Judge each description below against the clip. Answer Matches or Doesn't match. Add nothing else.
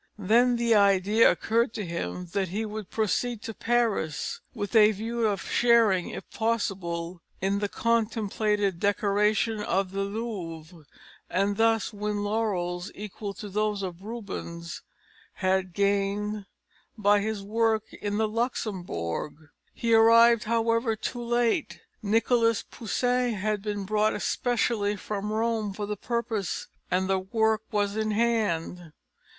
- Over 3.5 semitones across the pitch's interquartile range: Doesn't match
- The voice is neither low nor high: Doesn't match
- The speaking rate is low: Matches